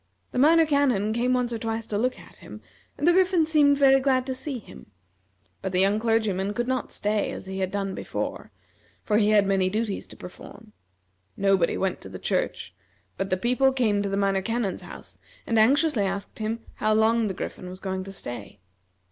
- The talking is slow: No, fast, 205 wpm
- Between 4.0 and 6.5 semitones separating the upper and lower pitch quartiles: Yes, average, 4.5 semitones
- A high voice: Yes, high, 215 Hz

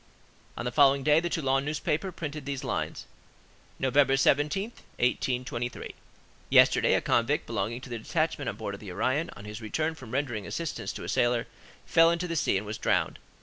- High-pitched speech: No, low, 135 Hz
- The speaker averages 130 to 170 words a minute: No, average, 185 wpm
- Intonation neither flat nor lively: Yes, average, 4.5 semitones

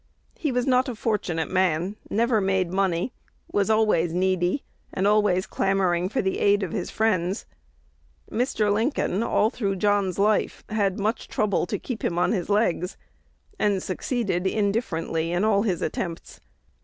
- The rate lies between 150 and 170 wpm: Yes, average, 155 wpm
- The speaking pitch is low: No, high, 200 Hz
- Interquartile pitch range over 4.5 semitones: No, average, 3.0 semitones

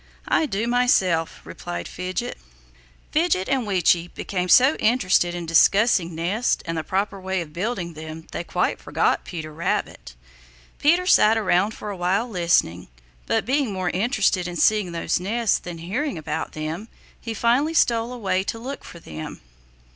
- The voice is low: No, high, 190 Hz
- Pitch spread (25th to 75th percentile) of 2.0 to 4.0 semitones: No, wide, 5.5 semitones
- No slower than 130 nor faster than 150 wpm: No, average, 160 wpm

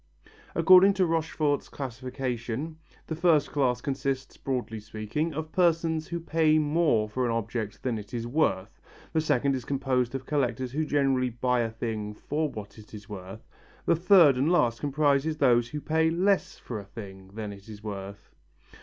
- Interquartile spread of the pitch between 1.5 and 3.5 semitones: No, wide, 5.6 semitones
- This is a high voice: No, low, 130 Hz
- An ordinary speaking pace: Yes, average, 170 wpm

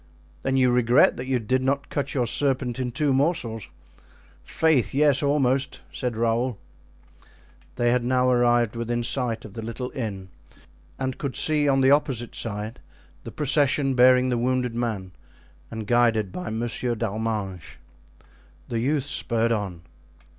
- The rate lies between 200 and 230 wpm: No, average, 145 wpm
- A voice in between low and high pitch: No, low, 125 Hz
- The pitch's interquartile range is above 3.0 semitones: No, narrow, 2.6 semitones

